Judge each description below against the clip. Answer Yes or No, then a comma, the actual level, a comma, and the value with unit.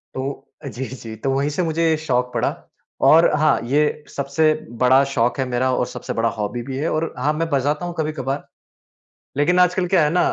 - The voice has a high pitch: No, medium, 140 Hz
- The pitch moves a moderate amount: Yes, average, 3.4 semitones